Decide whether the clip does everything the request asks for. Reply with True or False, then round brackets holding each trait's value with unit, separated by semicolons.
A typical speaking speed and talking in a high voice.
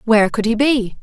False (235 wpm; 230 Hz)